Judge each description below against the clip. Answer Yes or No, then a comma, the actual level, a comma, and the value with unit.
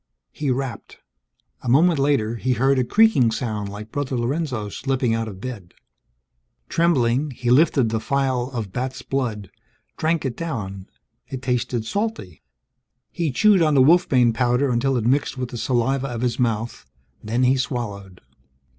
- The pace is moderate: Yes, average, 155 wpm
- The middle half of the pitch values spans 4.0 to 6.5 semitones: No, average, 3.2 semitones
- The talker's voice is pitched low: Yes, low, 125 Hz